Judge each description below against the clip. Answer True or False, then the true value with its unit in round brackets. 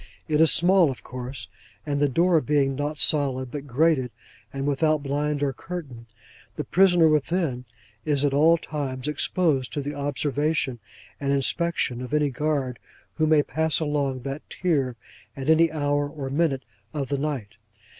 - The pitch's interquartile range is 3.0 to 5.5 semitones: False (2.5 semitones)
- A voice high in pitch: False (145 Hz)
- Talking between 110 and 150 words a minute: False (160 wpm)